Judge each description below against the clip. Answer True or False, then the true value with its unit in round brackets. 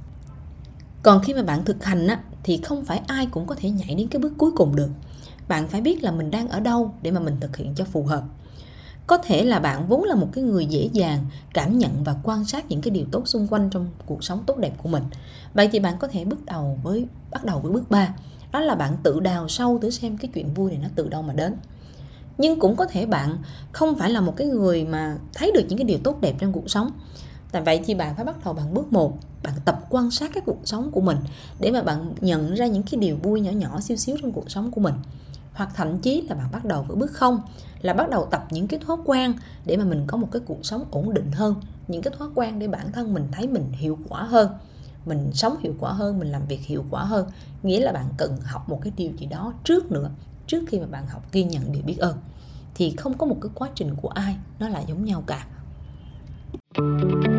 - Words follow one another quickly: True (255 wpm)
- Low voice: False (190 Hz)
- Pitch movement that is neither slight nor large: False (7.0 semitones)